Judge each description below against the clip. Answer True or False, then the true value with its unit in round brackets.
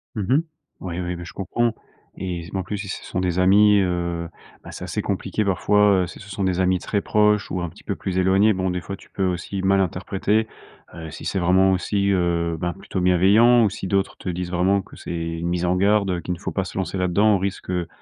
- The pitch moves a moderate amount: False (2.0 semitones)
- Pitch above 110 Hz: False (95 Hz)